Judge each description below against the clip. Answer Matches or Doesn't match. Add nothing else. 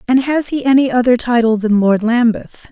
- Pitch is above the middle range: Matches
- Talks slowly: Doesn't match